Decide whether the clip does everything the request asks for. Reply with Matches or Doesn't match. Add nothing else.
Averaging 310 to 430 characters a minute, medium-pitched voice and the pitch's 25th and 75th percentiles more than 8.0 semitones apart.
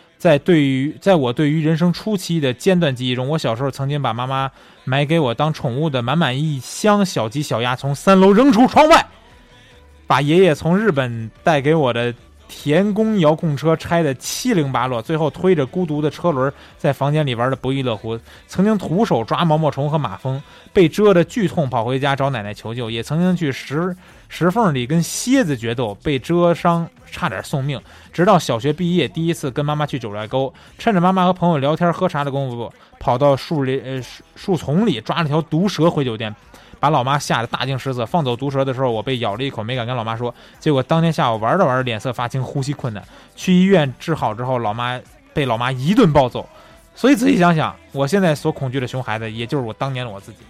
Doesn't match